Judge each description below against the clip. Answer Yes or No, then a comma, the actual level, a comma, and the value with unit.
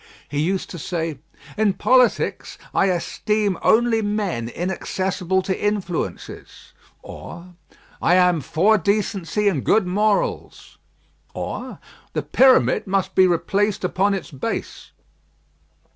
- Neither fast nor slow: No, slow, 115 wpm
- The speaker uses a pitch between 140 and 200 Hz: Yes, high, 190 Hz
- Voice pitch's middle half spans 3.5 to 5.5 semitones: No, average, 3.1 semitones